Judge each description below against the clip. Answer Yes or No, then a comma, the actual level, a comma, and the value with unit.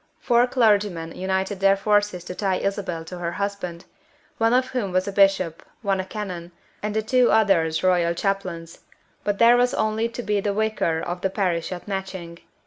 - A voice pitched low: No, high, 195 Hz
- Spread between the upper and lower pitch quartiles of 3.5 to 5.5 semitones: No, average, 3.0 semitones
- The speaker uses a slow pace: No, average, 185 wpm